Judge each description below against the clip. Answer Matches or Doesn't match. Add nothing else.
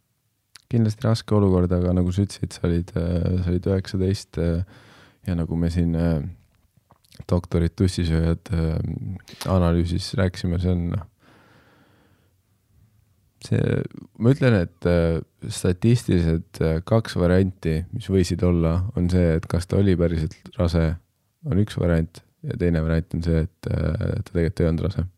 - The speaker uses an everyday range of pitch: Matches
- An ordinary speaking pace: Doesn't match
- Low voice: Matches